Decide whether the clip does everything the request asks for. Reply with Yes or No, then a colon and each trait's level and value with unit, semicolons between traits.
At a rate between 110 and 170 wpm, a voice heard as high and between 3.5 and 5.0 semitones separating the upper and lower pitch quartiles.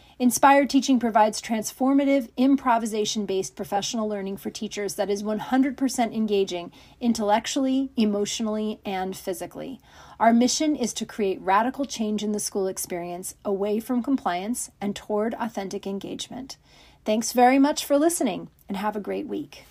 Yes: average, 140 wpm; high, 215 Hz; average, 3.8 semitones